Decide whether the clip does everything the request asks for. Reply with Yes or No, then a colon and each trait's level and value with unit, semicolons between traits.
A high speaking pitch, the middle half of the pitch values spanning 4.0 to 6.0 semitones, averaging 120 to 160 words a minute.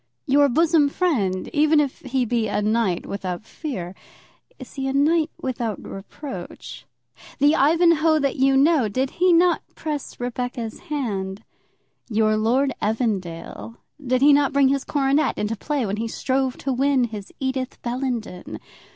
Yes: very high, 260 Hz; average, 4.6 semitones; average, 150 wpm